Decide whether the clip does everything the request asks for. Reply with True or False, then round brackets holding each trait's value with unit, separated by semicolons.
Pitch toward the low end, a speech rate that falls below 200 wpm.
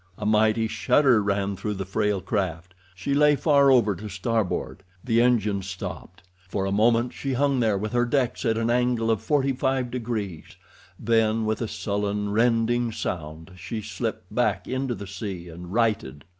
True (110 Hz; 170 wpm)